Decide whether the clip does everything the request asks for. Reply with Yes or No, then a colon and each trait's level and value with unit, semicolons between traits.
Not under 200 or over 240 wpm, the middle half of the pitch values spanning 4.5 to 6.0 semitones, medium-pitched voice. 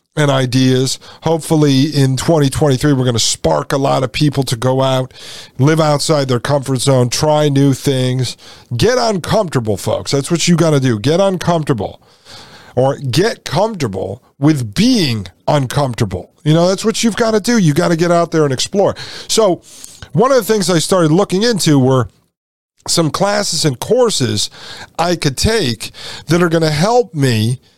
No: average, 175 wpm; average, 4.9 semitones; medium, 145 Hz